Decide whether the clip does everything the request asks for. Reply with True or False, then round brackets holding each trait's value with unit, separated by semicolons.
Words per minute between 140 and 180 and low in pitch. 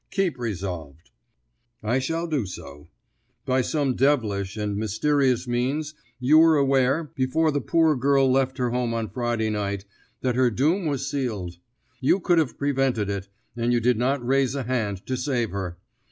True (170 wpm; 125 Hz)